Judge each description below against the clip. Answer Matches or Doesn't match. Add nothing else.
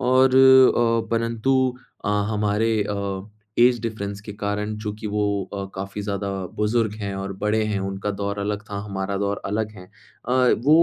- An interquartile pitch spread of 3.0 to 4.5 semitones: Doesn't match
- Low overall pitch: Matches